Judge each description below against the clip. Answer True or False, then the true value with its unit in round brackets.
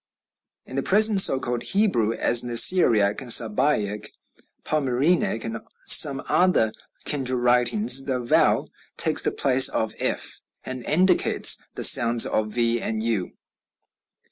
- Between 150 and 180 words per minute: False (135 wpm)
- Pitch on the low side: True (125 Hz)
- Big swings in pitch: False (4.5 semitones)